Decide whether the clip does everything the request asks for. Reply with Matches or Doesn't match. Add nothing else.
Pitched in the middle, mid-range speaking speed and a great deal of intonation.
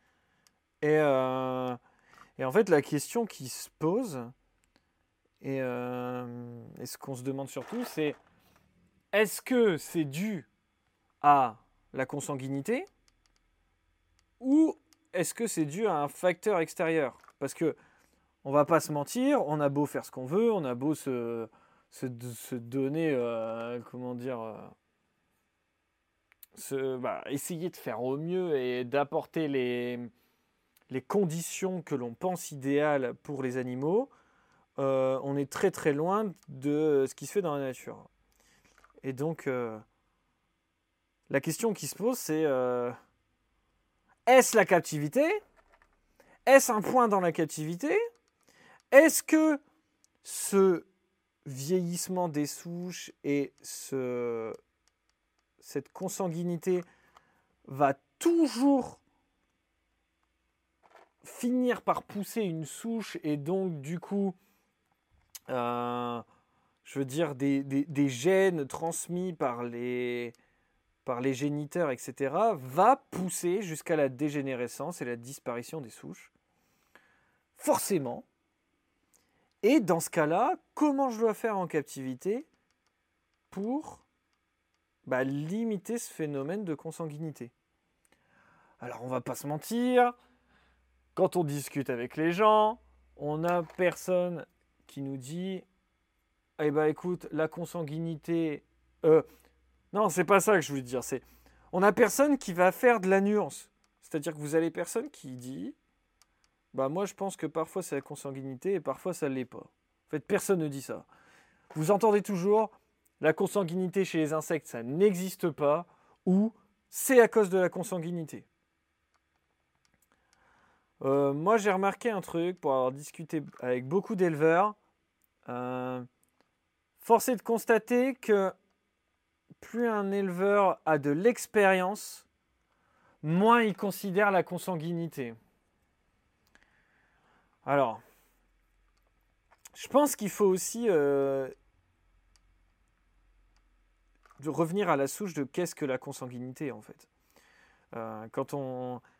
Doesn't match